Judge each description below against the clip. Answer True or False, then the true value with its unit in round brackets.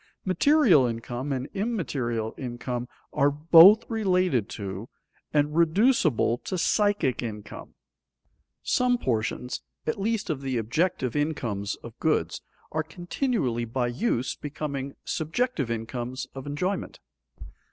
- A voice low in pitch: False (145 Hz)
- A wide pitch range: True (7.3 semitones)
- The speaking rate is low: True (110 wpm)